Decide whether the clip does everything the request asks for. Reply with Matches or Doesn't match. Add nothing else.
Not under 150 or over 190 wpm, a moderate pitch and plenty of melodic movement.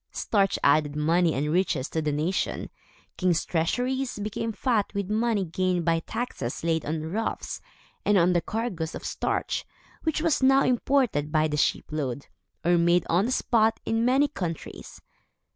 Matches